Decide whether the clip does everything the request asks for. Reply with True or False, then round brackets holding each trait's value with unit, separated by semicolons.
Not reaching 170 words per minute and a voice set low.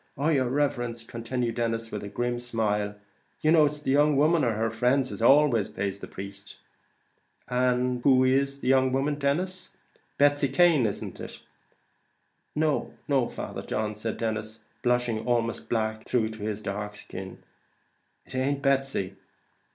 True (150 wpm; 120 Hz)